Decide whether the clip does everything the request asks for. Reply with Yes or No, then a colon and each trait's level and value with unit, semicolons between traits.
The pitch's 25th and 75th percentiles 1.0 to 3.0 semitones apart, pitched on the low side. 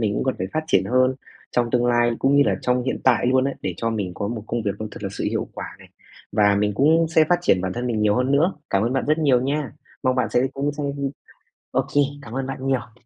No: average, 4.0 semitones; low, 125 Hz